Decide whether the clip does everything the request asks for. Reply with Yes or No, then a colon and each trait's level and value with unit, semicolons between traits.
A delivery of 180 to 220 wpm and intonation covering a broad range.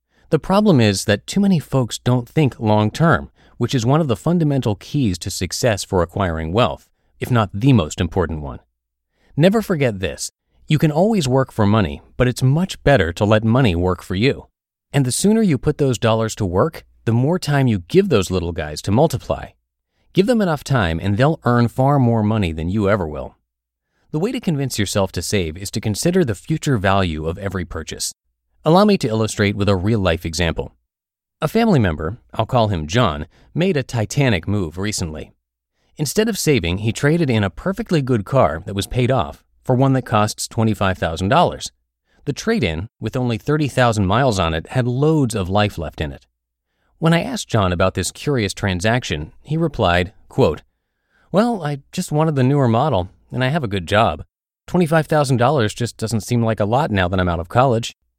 Yes: average, 195 wpm; wide, 7.1 semitones